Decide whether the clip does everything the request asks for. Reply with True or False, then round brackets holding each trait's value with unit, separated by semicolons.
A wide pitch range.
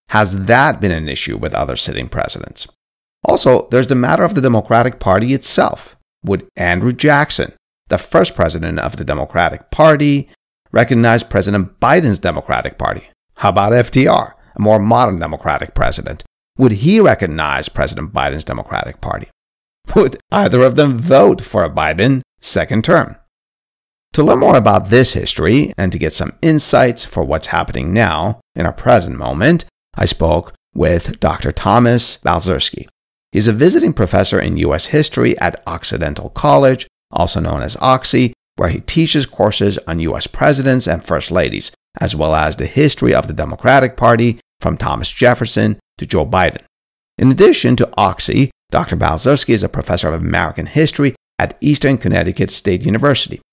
True (6.5 semitones)